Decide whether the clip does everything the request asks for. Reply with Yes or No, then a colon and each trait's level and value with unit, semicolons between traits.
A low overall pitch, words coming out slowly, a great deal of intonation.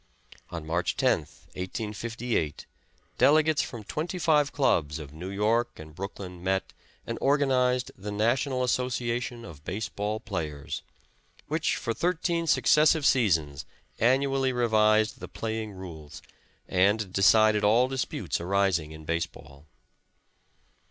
Yes: low, 110 Hz; slow, 120 wpm; wide, 6.2 semitones